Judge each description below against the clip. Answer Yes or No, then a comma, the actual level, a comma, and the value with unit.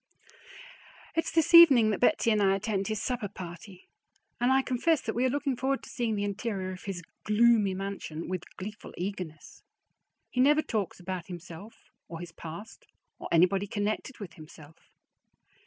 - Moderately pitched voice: No, high, 205 Hz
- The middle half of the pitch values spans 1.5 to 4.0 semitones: No, average, 4.6 semitones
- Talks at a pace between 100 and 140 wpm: No, average, 165 wpm